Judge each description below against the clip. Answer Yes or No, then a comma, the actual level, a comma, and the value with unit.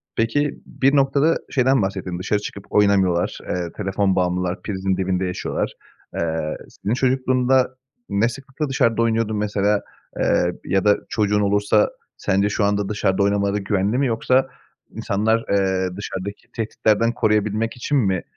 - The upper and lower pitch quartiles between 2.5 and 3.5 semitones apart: Yes, average, 3.2 semitones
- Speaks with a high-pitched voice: No, low, 105 Hz